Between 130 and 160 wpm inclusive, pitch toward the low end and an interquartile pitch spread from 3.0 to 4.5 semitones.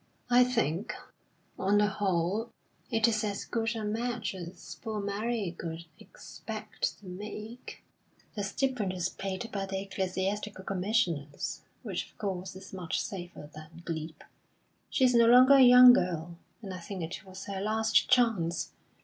No: average, 155 wpm; high, 200 Hz; average, 3.8 semitones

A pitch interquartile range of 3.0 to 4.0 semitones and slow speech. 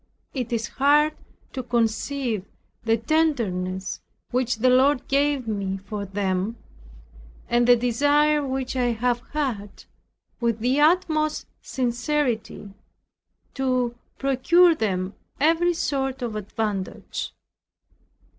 No: average, 4.6 semitones; slow, 105 wpm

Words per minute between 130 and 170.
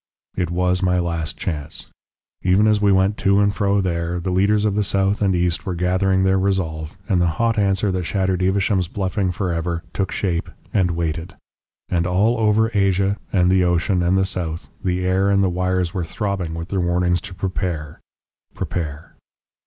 No: average, 185 wpm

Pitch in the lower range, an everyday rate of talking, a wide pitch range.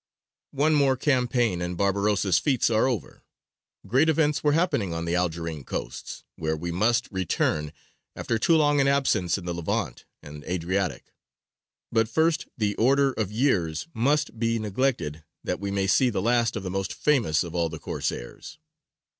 Yes: low, 105 Hz; average, 165 wpm; wide, 7.2 semitones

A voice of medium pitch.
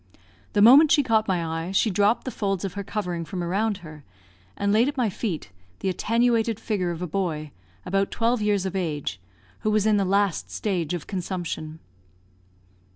No: high, 195 Hz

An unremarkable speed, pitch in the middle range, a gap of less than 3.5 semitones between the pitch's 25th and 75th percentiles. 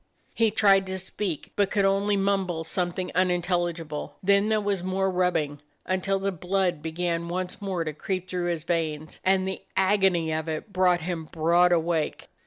Yes: average, 170 wpm; medium, 180 Hz; narrow, 2.5 semitones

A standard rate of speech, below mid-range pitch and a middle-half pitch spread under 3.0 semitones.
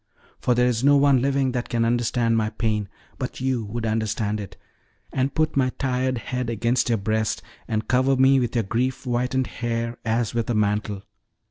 Yes: average, 190 wpm; low, 120 Hz; narrow, 2.6 semitones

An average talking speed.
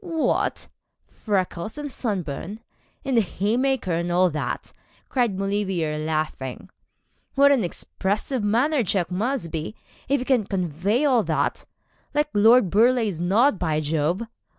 No: slow, 130 wpm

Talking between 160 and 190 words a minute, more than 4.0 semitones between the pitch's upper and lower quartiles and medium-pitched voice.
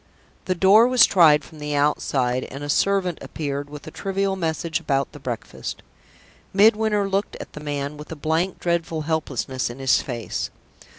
Yes: average, 170 wpm; average, 5.1 semitones; medium, 155 Hz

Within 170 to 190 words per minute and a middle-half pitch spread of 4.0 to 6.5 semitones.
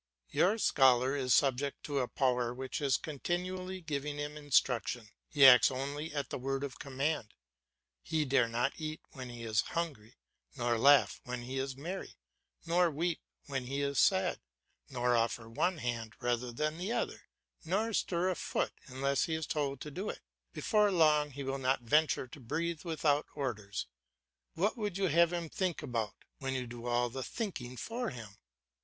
Yes: average, 175 wpm; average, 4.5 semitones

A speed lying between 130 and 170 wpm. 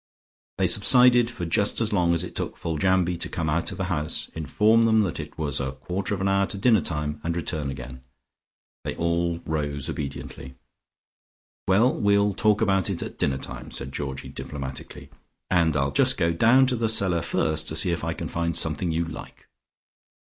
No: average, 190 wpm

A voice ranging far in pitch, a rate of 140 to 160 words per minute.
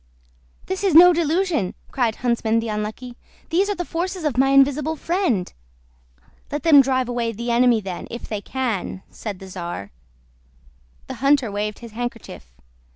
Yes: wide, 5.8 semitones; average, 155 wpm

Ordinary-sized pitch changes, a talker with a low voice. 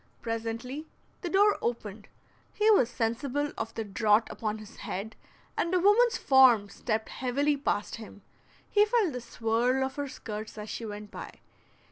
No: average, 4.8 semitones; high, 235 Hz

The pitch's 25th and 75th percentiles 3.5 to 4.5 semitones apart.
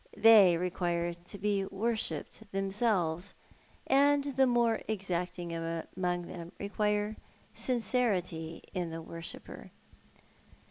Yes: average, 4.2 semitones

